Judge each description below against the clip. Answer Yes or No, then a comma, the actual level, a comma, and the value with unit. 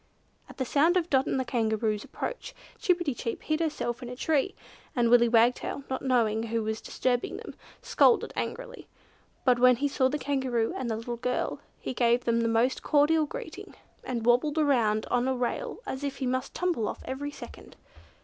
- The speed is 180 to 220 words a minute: Yes, average, 195 wpm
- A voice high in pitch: Yes, very high, 255 Hz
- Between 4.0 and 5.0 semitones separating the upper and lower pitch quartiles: No, average, 3.6 semitones